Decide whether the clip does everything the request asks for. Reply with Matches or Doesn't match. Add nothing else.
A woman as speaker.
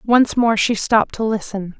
Matches